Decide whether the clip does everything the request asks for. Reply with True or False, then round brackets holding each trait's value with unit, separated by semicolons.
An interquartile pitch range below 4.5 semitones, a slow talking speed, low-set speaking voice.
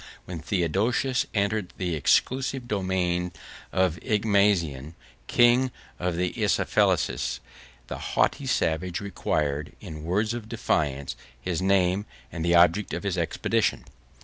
True (3.8 semitones; 120 wpm; 90 Hz)